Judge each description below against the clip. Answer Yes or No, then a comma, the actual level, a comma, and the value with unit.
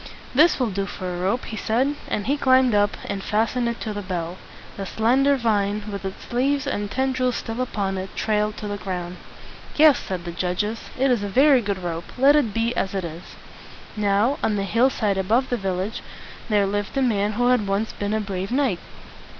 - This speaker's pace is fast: Yes, fast, 215 wpm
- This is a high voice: Yes, high, 210 Hz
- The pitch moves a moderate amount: Yes, average, 4.2 semitones